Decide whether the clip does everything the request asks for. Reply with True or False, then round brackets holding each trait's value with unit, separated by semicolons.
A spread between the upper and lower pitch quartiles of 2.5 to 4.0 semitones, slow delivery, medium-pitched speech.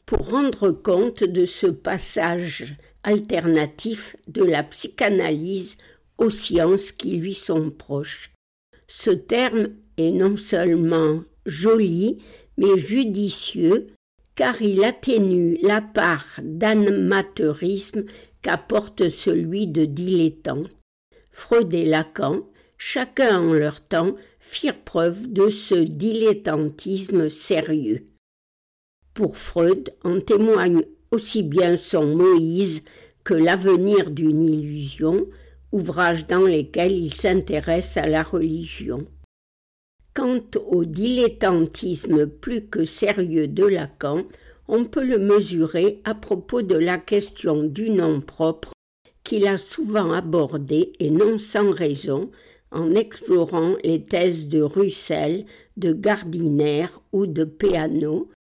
False (4.7 semitones; 110 wpm; 180 Hz)